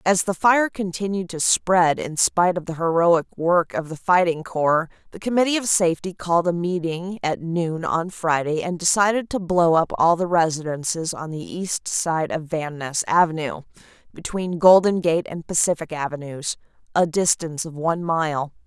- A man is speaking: No, female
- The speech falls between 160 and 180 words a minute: Yes, average, 175 wpm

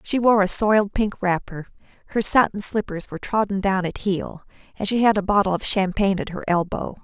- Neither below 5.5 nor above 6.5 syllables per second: Yes, 5.6 syllables/s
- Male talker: No, female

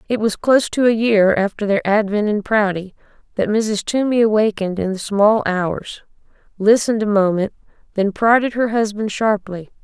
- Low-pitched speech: No, high, 210 Hz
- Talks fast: No, average, 165 wpm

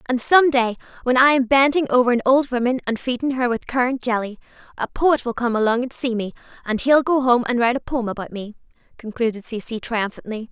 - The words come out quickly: Yes, fast, 215 wpm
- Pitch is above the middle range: Yes, high, 245 Hz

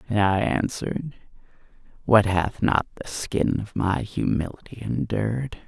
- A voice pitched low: Yes, low, 105 Hz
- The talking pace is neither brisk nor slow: No, slow, 125 wpm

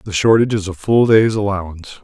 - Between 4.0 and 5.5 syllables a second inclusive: No, 6.0 syllables/s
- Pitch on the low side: Yes, low, 100 Hz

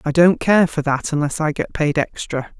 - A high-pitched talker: No, medium, 155 Hz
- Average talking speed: No, fast, 230 wpm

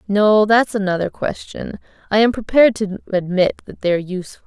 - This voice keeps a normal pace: Yes, average, 160 wpm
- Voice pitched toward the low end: No, high, 205 Hz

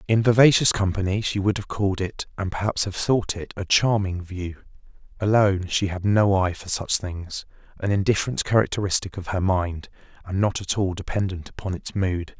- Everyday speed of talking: Yes, average, 180 wpm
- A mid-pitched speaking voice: No, very low, 95 Hz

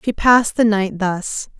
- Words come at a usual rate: Yes, average, 190 wpm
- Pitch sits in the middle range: No, high, 210 Hz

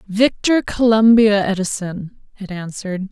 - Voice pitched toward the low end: No, high, 205 Hz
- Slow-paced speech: Yes, slow, 95 wpm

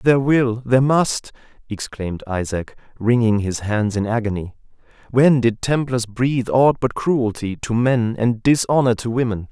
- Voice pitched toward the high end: No, low, 120 Hz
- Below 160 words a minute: Yes, average, 150 wpm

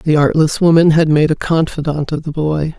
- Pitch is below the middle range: No, medium, 155 Hz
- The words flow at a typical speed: No, fast, 215 wpm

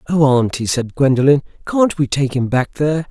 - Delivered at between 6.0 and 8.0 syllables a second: No, 5.3 syllables/s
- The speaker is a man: Yes, male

